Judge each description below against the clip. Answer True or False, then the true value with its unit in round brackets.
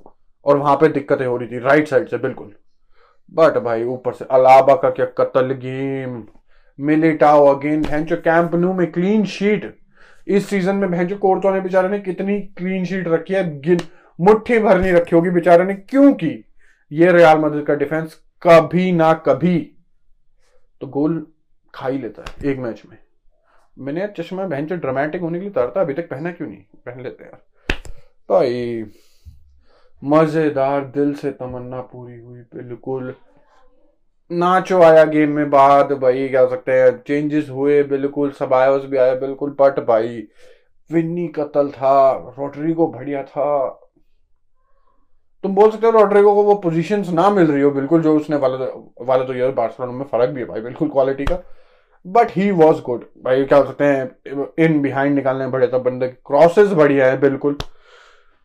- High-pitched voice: False (150 Hz)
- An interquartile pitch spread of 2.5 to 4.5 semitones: False (5.1 semitones)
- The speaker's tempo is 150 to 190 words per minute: False (140 wpm)